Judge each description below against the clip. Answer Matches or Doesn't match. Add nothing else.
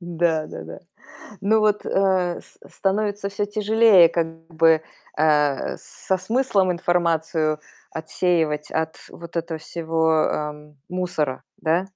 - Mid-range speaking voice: Matches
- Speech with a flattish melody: Doesn't match